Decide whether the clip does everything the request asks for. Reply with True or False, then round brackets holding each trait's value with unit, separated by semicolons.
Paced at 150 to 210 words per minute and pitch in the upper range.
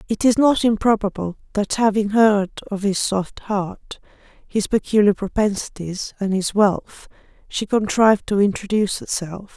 False (140 wpm; 205 Hz)